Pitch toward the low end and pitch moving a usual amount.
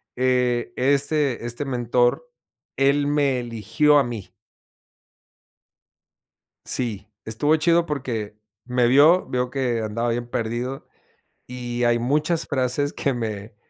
Yes: low, 125 Hz; average, 3.1 semitones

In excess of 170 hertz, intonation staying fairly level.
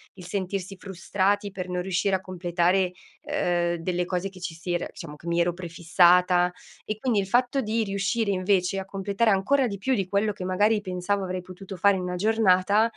Yes: high, 190 Hz; narrow, 2.1 semitones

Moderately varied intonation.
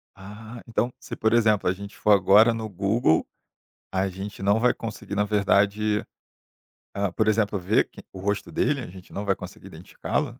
No: narrow, 2.1 semitones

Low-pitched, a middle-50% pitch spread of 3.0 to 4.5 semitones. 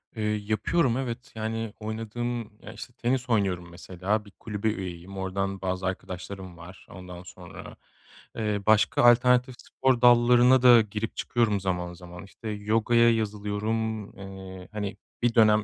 Yes: low, 105 Hz; average, 3.6 semitones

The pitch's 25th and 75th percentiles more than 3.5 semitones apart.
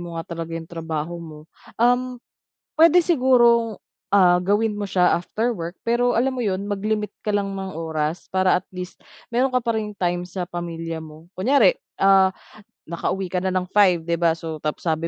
Yes: average, 4.6 semitones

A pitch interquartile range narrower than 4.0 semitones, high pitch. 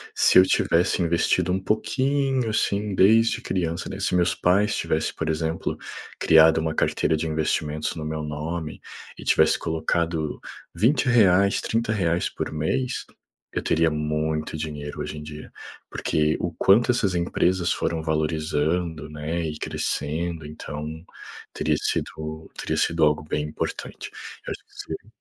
No: average, 3.2 semitones; very low, 80 Hz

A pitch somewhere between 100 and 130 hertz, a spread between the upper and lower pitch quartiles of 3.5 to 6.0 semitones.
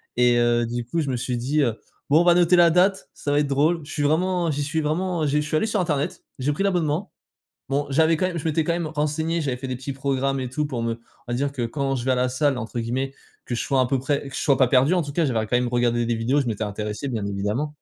No: medium, 140 Hz; average, 4.2 semitones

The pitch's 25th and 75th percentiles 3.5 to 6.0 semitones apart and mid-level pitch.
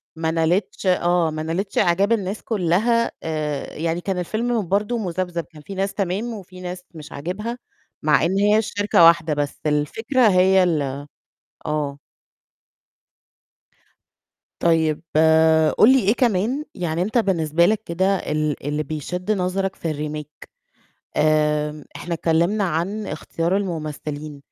Yes: average, 4.4 semitones; medium, 175 Hz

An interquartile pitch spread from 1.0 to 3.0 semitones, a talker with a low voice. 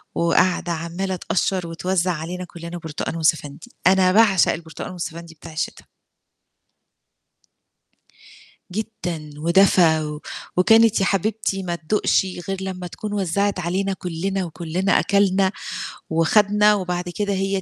No: narrow, 2.6 semitones; medium, 180 Hz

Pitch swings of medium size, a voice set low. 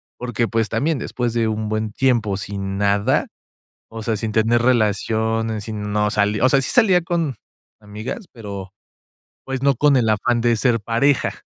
Yes: average, 3.0 semitones; low, 115 Hz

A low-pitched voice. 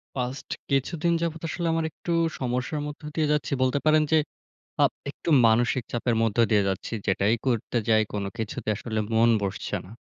Yes: low, 125 Hz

